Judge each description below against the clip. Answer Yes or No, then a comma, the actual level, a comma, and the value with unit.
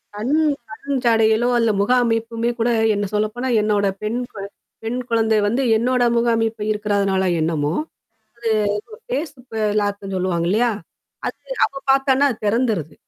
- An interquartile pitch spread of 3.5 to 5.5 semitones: No, average, 2.9 semitones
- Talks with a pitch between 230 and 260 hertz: No, high, 220 Hz